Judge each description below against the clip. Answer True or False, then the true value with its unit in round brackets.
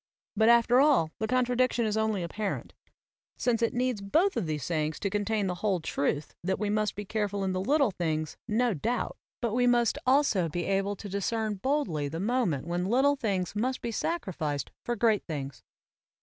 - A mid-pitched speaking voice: False (210 Hz)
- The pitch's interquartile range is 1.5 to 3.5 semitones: False (5.0 semitones)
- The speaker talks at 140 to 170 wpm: False (185 wpm)